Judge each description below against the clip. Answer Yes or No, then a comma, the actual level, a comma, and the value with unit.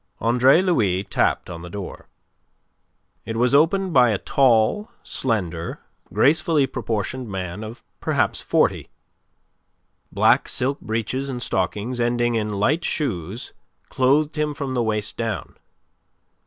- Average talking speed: No, slow, 125 wpm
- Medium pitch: No, low, 120 Hz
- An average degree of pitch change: Yes, average, 4.7 semitones